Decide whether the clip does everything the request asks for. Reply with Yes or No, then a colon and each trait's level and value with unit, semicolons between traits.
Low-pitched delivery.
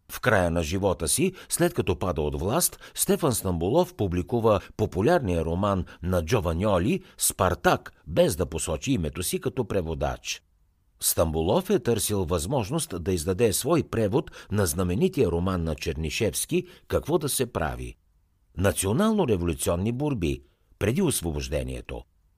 Yes: very low, 95 Hz